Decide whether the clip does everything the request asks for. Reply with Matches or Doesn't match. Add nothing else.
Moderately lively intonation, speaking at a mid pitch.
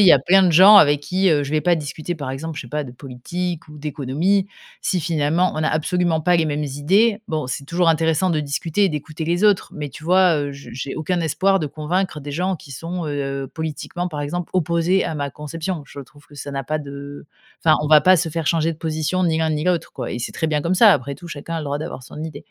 Matches